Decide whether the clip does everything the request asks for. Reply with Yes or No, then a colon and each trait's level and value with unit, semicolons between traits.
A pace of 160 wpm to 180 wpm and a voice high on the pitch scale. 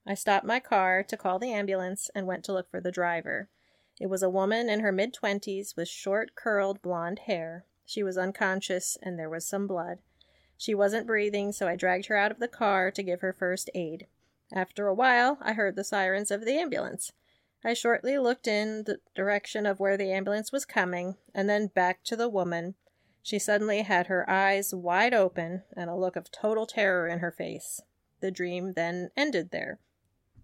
No: average, 200 wpm; high, 195 Hz